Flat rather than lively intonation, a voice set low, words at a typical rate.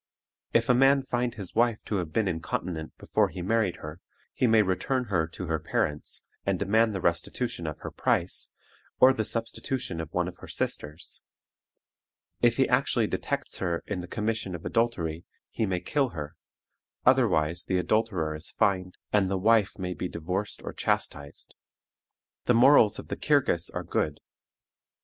No: average, 5.1 semitones; very low, 95 Hz; average, 170 wpm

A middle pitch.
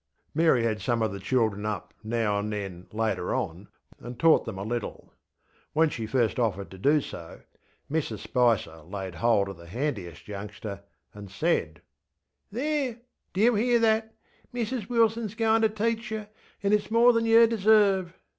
No: low, 125 Hz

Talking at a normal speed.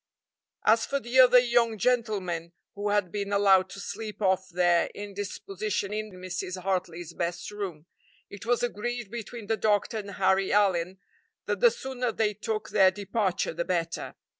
Yes: average, 160 wpm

